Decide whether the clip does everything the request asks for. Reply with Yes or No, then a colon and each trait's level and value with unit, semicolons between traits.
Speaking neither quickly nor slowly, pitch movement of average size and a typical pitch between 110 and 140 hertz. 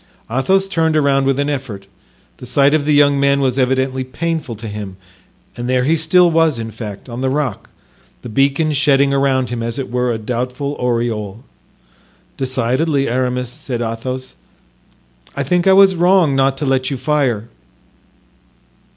Yes: average, 165 wpm; average, 3.1 semitones; low, 135 Hz